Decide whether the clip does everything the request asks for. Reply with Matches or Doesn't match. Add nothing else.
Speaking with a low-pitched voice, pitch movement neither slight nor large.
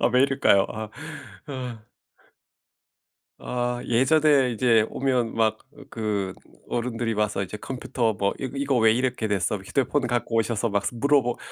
Matches